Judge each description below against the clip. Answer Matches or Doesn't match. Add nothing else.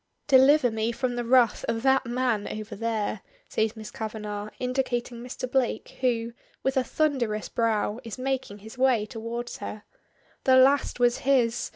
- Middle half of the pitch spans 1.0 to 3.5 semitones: Matches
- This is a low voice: Doesn't match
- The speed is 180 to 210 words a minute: Doesn't match